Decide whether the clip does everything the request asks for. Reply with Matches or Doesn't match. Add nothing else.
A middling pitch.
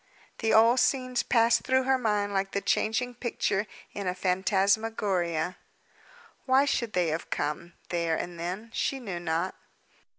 Doesn't match